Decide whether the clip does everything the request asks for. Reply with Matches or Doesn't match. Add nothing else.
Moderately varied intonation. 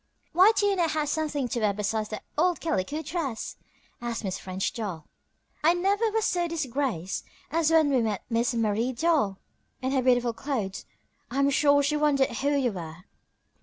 Doesn't match